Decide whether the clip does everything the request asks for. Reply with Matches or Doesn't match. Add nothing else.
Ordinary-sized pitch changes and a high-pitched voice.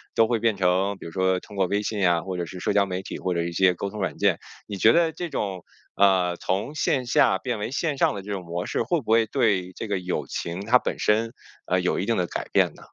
Doesn't match